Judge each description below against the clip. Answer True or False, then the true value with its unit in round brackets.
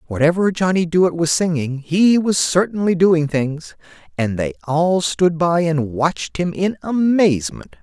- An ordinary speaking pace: True (155 wpm)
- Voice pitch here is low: False (165 Hz)